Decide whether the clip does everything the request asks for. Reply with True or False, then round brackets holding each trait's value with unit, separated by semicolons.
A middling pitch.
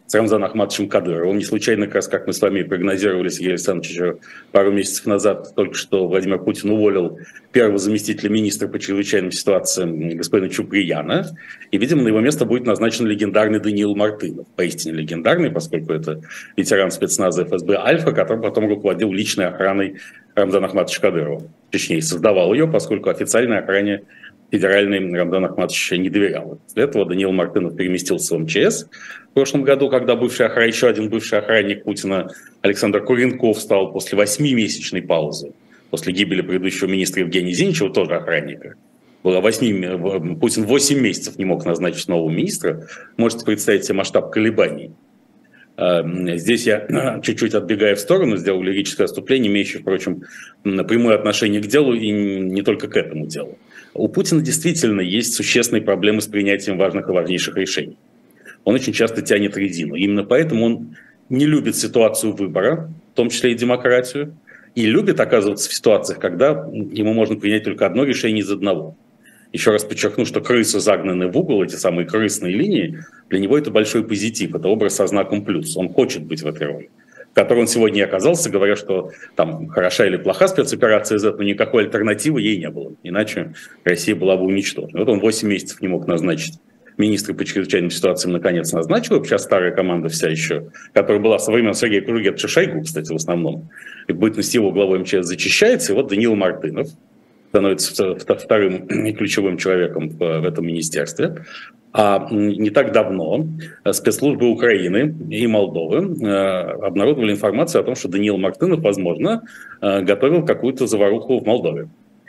False (100 Hz)